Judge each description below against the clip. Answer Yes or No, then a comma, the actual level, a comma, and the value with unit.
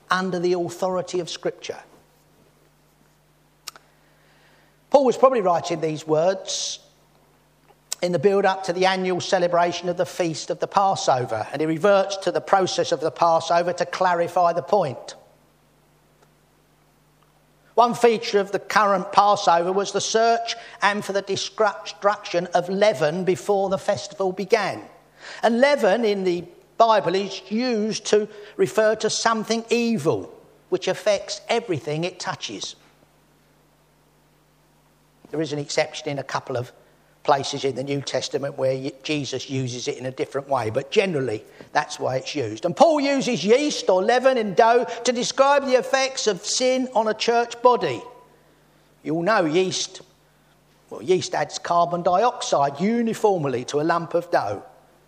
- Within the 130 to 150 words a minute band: Yes, average, 145 wpm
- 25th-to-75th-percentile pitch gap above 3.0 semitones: Yes, average, 4.9 semitones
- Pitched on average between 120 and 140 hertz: No, high, 195 Hz